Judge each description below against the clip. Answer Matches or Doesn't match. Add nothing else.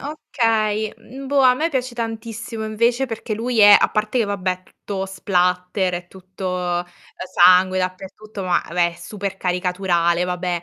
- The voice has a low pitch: Doesn't match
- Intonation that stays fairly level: Doesn't match